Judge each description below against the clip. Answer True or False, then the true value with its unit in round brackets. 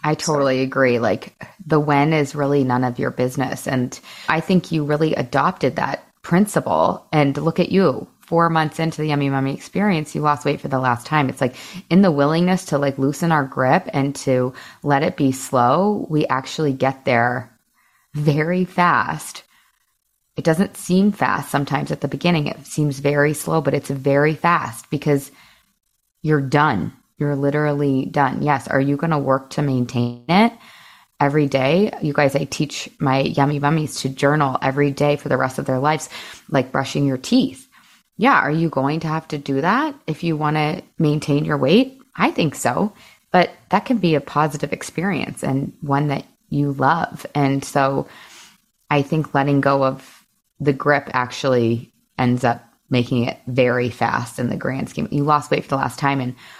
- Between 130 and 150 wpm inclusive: False (185 wpm)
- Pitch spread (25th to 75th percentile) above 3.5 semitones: False (2.9 semitones)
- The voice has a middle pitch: True (145 Hz)